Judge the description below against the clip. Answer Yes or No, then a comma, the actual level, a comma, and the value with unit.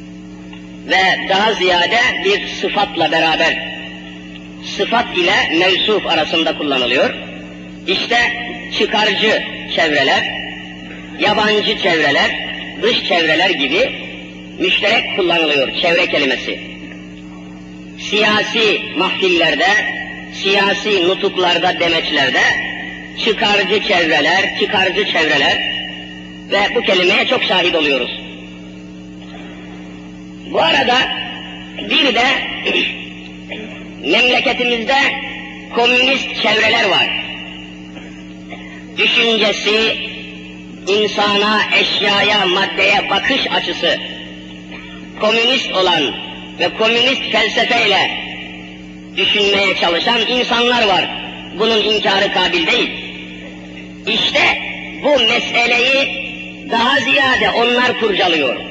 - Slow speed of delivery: Yes, slow, 75 wpm